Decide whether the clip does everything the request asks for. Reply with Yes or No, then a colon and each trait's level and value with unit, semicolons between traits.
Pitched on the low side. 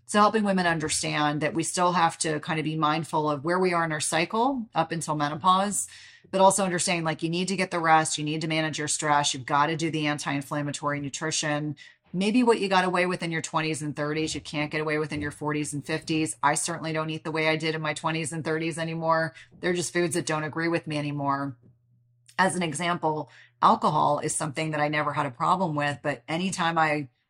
No: medium, 155 Hz